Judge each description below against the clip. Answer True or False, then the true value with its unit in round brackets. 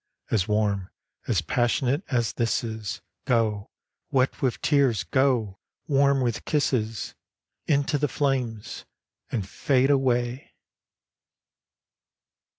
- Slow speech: True (100 wpm)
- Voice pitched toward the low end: True (120 Hz)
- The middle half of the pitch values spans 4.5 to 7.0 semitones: False (3.8 semitones)